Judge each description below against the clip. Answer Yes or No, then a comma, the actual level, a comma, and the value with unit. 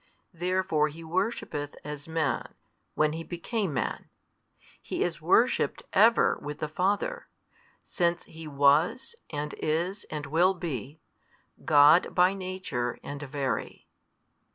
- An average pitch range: Yes, average, 3.9 semitones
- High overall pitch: No, medium, 160 Hz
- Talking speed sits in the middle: No, slow, 120 wpm